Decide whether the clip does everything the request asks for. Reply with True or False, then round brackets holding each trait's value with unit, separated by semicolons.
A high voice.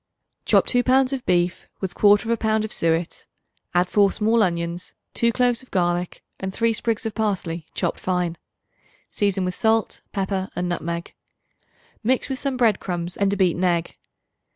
True (195 Hz)